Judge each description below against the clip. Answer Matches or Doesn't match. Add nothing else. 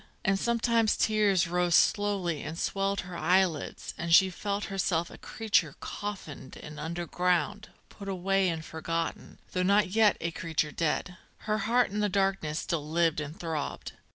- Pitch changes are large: Doesn't match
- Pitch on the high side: Doesn't match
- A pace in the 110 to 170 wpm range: Matches